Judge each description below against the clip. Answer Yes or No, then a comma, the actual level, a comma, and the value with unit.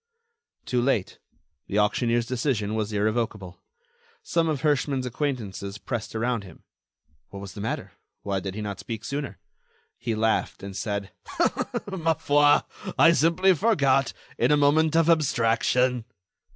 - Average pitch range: No, wide, 5.7 semitones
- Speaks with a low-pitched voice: Yes, low, 120 Hz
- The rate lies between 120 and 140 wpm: Yes, slow, 135 wpm